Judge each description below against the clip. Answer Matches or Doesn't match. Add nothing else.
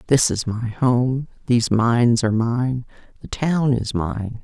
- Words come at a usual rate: Matches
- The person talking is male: Doesn't match